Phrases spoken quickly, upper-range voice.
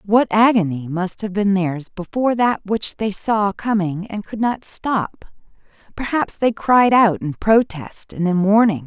No: average, 170 wpm; high, 205 Hz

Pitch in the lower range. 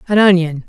No: medium, 180 Hz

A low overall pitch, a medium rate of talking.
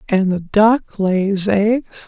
No: high, 205 Hz; average, 145 wpm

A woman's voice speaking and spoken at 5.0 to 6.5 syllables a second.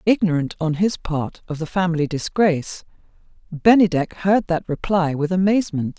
Yes: female; 5.1 syllables/s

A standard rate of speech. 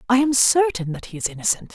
No: fast, 240 wpm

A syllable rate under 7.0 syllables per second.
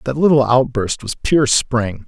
Yes: 4.1 syllables/s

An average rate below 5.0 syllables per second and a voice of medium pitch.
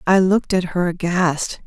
Yes: 4.6 syllables/s; medium, 180 Hz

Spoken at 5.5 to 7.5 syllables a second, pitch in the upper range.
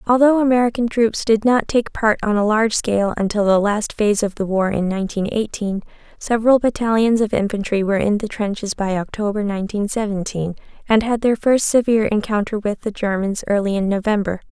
Yes: 5.8 syllables/s; high, 210 Hz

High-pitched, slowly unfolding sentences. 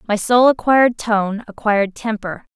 Yes: high, 220 Hz; slow, 120 wpm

